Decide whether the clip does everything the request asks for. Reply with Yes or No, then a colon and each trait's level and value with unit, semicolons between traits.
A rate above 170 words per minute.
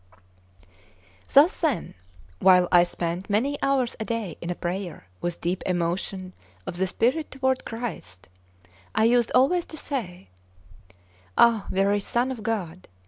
No: slow, 135 wpm